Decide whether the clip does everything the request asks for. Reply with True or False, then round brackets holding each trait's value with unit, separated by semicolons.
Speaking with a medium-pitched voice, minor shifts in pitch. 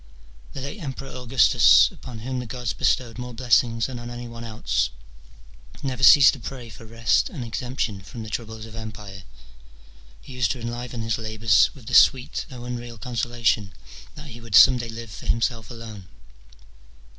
False (115 Hz; 1.9 semitones)